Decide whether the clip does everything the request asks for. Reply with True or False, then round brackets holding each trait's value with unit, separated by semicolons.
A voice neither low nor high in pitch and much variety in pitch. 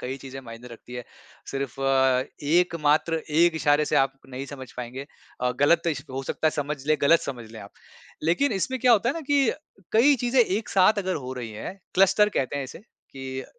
True (145 Hz; 6.2 semitones)